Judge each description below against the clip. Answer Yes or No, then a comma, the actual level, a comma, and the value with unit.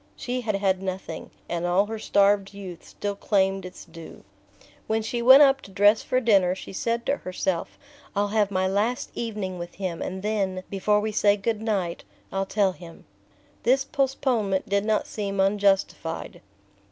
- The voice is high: Yes, high, 200 Hz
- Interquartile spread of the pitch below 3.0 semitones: Yes, narrow, 2.6 semitones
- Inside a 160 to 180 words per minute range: Yes, average, 170 wpm